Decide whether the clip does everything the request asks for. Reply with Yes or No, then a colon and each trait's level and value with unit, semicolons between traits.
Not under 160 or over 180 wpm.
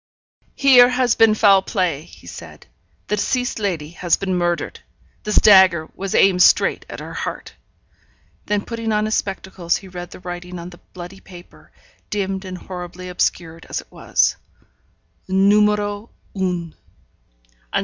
No: average, 145 wpm